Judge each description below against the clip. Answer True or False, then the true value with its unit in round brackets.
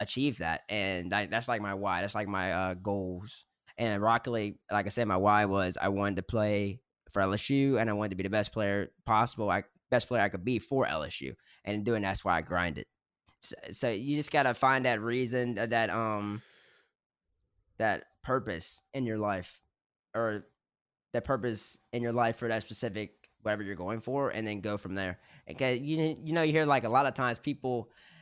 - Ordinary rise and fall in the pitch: True (3.5 semitones)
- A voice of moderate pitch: False (110 Hz)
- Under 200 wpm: False (205 wpm)